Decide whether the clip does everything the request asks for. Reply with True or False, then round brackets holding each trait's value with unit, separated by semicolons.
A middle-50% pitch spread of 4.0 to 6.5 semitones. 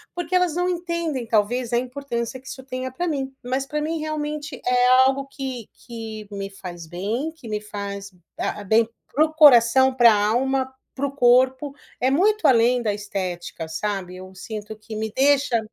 True (4.7 semitones)